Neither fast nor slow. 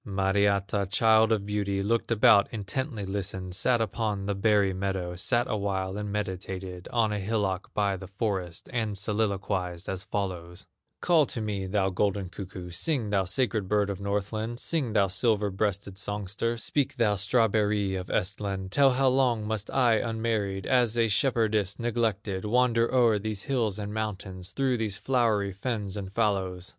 Yes: average, 160 wpm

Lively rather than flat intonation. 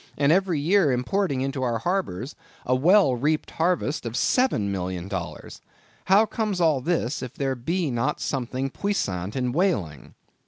Yes: wide, 6.9 semitones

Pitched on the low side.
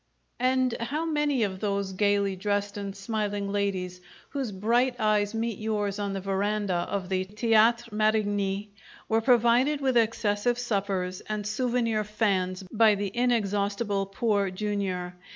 No: high, 210 Hz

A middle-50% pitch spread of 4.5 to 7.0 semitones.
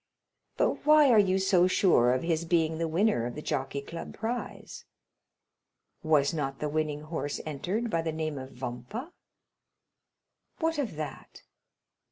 Yes: average, 5.1 semitones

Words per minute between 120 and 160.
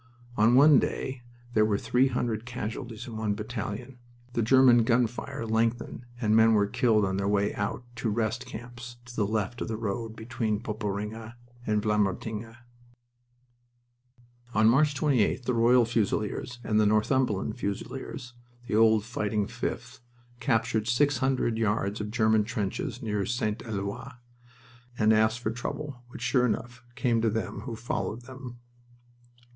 Yes: average, 150 wpm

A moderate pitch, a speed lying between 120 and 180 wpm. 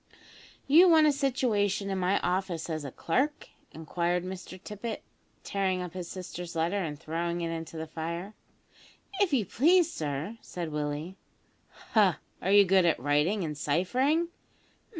Yes: medium, 180 Hz; average, 150 wpm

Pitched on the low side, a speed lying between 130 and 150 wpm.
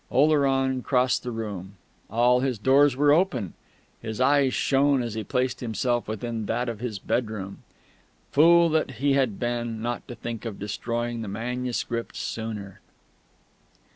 Yes: low, 120 Hz; average, 145 wpm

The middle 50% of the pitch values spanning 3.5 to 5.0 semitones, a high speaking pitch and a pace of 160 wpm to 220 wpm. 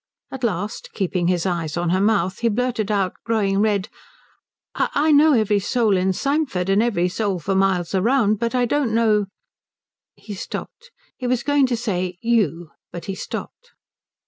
Yes: average, 4.4 semitones; high, 210 Hz; average, 170 wpm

